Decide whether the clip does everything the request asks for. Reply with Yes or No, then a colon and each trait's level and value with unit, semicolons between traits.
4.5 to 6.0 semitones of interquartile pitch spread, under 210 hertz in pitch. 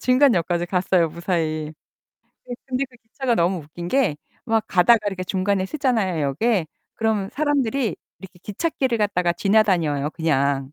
Yes: wide, 5.6 semitones; high, 190 Hz